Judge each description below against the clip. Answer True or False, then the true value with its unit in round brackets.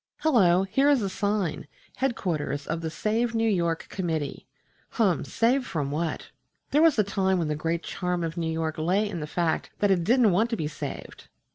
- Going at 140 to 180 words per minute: False (195 wpm)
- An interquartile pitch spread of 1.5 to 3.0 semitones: False (5.3 semitones)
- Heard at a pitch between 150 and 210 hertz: True (185 Hz)